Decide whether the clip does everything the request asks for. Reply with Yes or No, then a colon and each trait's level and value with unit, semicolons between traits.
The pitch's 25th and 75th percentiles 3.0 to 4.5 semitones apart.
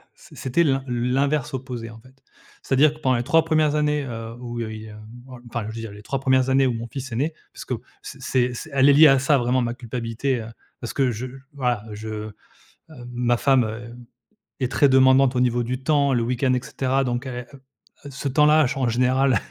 No: narrow, 2.4 semitones